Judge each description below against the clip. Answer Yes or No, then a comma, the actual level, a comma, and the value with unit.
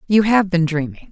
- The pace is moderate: No, fast, 215 wpm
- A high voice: No, medium, 180 Hz